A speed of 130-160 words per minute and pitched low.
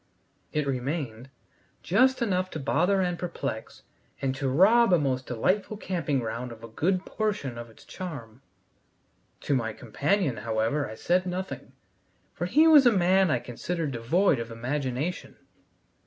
No: average, 150 wpm; medium, 145 Hz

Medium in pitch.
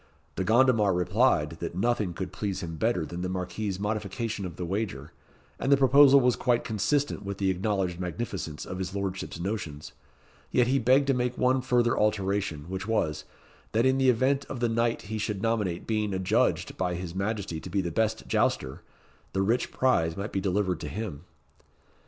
No: low, 100 Hz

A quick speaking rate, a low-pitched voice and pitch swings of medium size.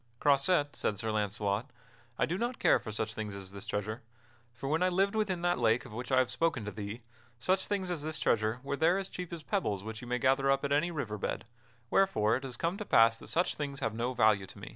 No: fast, 250 wpm; low, 130 Hz; wide, 7.4 semitones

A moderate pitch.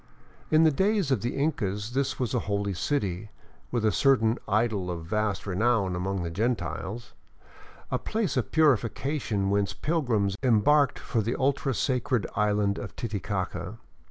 No: low, 110 Hz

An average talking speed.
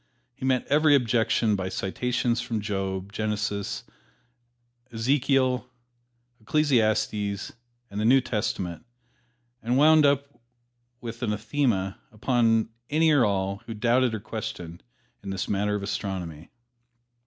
No: slow, 120 wpm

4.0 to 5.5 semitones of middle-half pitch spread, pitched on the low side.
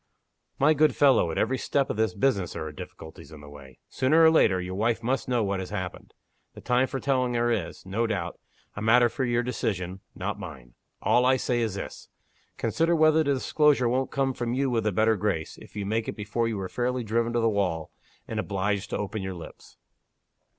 Yes: average, 4.8 semitones; low, 115 Hz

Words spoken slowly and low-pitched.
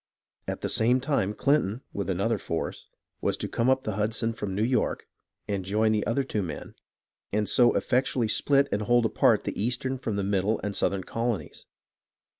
No: average, 185 wpm; low, 110 Hz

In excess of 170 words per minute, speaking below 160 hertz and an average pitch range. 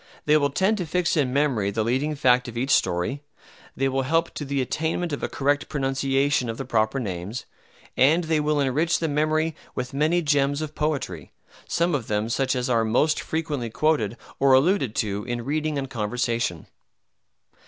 Yes: average, 185 wpm; low, 135 Hz; average, 4.2 semitones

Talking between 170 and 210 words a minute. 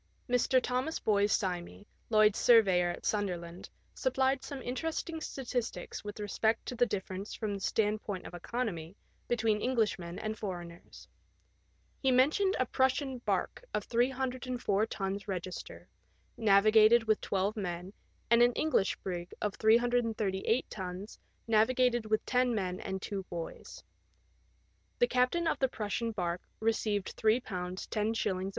No: slow, 135 wpm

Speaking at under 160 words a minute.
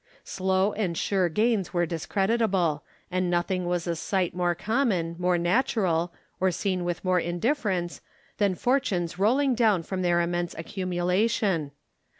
Yes: average, 140 wpm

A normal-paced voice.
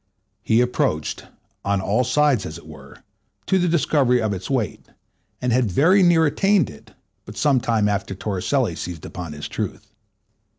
Yes: average, 165 wpm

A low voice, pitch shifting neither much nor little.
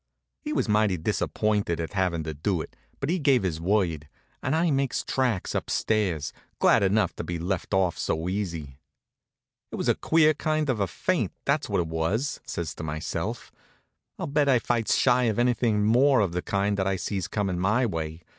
No: low, 100 Hz; wide, 6.4 semitones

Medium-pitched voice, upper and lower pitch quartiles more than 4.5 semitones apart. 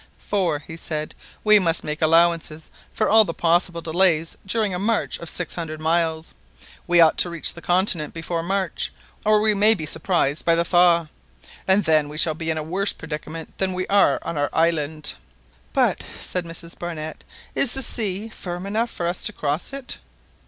No: medium, 170 Hz; average, 3.1 semitones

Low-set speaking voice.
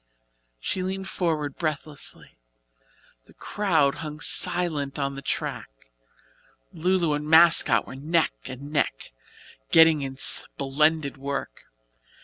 No: medium, 150 Hz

